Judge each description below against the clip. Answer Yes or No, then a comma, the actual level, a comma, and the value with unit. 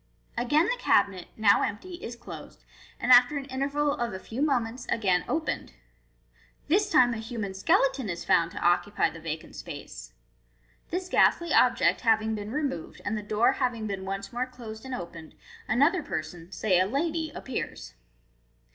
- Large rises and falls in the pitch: Yes, wide, 5.9 semitones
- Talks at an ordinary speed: Yes, average, 175 wpm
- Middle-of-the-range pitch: No, high, 235 Hz